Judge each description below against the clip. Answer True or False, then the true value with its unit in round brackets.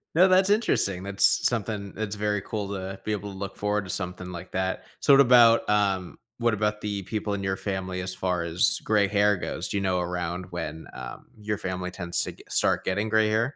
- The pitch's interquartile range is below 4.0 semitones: True (2.5 semitones)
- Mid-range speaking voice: False (100 Hz)